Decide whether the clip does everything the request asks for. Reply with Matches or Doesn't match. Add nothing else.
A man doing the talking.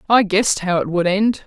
Doesn't match